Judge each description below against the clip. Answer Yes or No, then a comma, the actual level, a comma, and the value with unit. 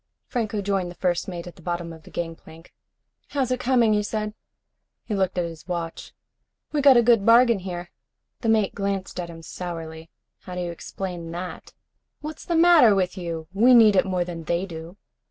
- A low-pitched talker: No, medium, 185 Hz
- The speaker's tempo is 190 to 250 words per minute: Yes, average, 195 wpm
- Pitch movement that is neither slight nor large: Yes, average, 4.4 semitones